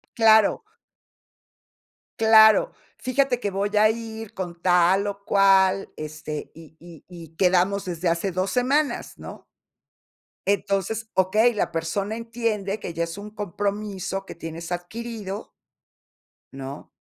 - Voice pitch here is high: Yes, high, 195 Hz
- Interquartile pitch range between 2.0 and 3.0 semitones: No, average, 3.7 semitones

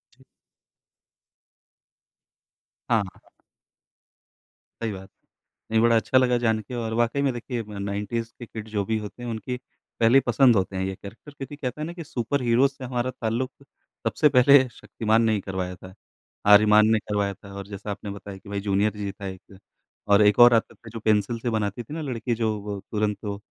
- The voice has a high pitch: No, low, 110 Hz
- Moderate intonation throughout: Yes, average, 3.1 semitones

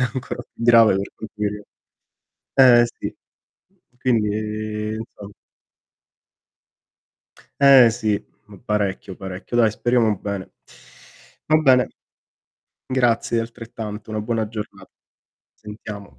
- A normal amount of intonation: No, narrow, 2.3 semitones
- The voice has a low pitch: Yes, low, 110 Hz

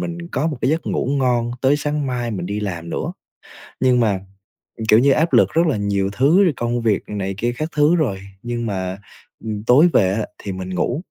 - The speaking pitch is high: No, low, 120 Hz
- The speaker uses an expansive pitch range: Yes, wide, 6.4 semitones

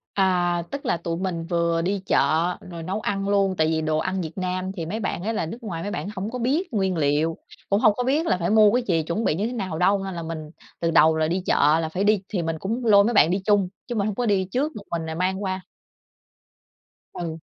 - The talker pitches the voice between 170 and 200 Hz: Yes, medium, 185 Hz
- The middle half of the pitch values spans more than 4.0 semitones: No, average, 3.7 semitones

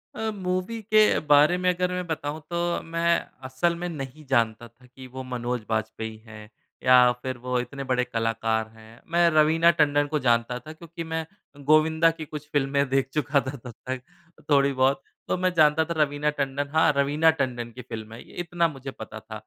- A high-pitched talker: No, medium, 140 Hz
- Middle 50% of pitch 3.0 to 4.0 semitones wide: No, average, 4.6 semitones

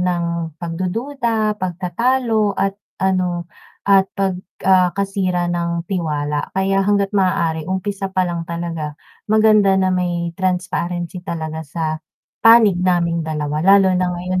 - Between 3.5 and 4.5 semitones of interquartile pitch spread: No, narrow, 2.5 semitones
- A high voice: No, medium, 180 Hz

